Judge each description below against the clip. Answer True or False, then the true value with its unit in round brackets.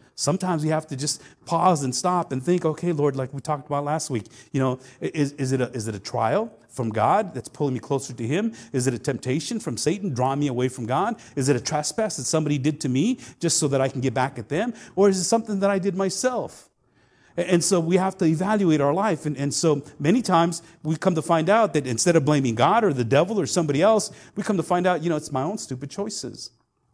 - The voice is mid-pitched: True (150 Hz)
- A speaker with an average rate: False (255 wpm)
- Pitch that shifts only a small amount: False (5.2 semitones)